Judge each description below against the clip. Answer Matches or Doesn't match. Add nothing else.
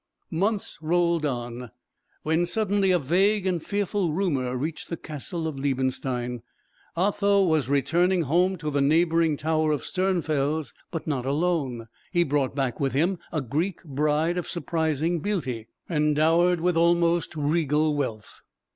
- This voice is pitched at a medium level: Matches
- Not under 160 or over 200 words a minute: Doesn't match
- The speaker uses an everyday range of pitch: Matches